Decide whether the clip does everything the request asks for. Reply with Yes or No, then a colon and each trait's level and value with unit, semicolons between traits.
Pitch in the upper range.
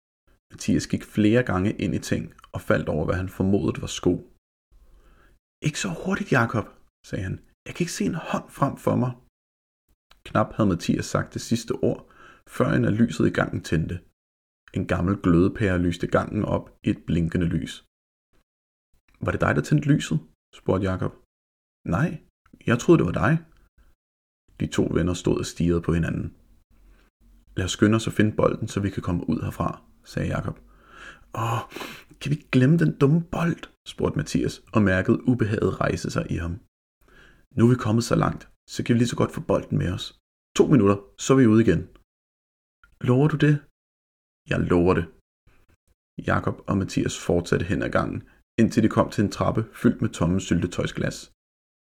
No: very low, 95 Hz